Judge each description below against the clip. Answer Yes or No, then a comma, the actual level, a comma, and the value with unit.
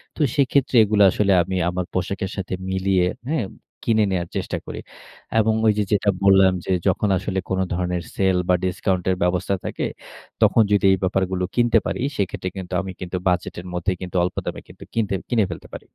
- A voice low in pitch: Yes, very low, 95 Hz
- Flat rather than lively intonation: Yes, narrow, 2.1 semitones